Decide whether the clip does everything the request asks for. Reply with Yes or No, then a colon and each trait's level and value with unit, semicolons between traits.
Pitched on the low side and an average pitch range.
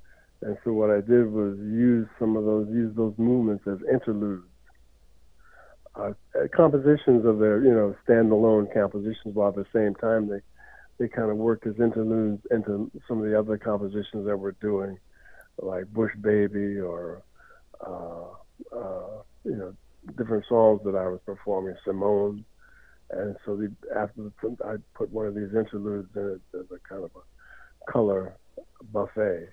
No: low, 105 Hz; narrow, 1.8 semitones